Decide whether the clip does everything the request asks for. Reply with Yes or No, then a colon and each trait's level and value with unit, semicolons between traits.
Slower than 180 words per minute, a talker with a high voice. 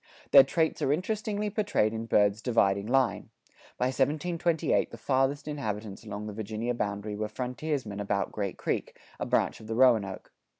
No: average, 160 wpm; low, 115 Hz